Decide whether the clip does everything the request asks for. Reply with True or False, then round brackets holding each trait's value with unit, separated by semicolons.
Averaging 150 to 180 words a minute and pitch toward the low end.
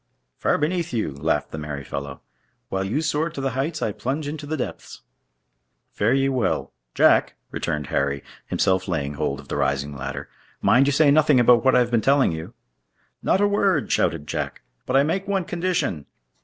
False (190 wpm; 125 Hz)